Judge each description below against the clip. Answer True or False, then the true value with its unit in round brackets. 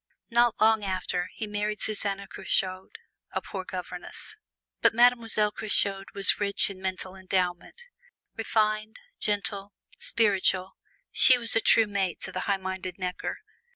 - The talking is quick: False (135 wpm)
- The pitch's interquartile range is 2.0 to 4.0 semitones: True (2.5 semitones)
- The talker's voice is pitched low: False (200 Hz)